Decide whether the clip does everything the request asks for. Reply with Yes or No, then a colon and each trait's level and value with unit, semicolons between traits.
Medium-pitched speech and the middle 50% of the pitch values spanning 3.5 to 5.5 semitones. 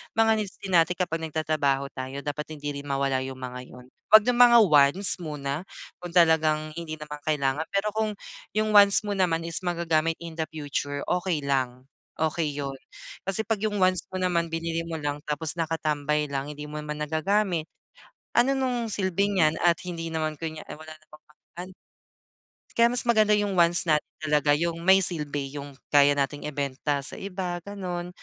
Yes: medium, 160 Hz; average, 4.0 semitones